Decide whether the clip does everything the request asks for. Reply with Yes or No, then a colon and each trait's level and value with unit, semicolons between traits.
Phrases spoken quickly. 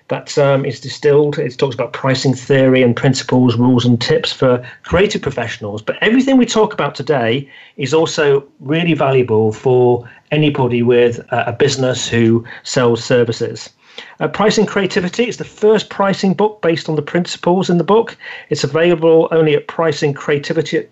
No: average, 165 wpm